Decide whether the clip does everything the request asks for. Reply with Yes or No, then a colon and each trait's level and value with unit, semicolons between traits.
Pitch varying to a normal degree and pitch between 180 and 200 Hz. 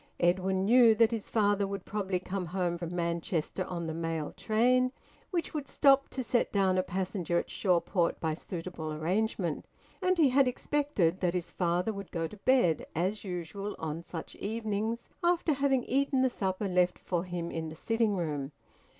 Yes: average, 4.9 semitones; high, 190 Hz